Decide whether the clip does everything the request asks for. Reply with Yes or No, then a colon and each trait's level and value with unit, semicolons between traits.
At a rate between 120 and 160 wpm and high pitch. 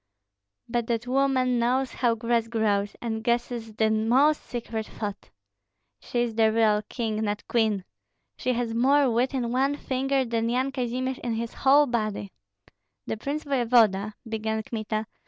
Yes: average, 155 wpm; high, 235 Hz